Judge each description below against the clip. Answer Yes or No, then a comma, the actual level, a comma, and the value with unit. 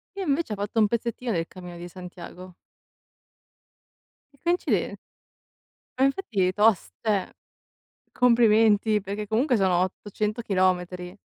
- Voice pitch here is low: No, high, 210 Hz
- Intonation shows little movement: No, average, 4.1 semitones